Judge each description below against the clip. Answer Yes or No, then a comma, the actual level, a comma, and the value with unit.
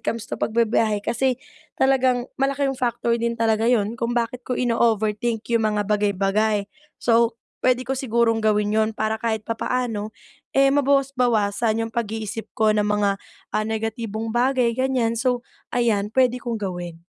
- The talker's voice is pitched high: Yes, high, 230 Hz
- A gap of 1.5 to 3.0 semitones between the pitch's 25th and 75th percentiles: Yes, narrow, 2.4 semitones